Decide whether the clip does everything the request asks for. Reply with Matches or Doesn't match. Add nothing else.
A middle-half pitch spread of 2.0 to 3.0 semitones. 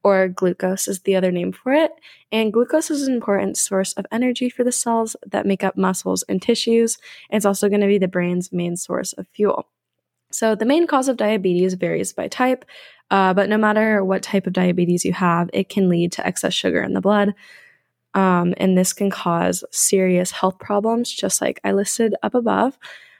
Doesn't match